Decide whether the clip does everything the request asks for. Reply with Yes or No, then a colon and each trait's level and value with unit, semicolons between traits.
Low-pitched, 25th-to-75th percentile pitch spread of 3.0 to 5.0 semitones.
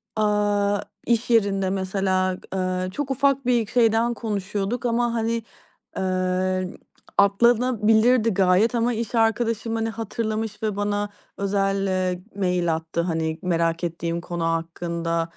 No: high, 200 Hz; average, 3.7 semitones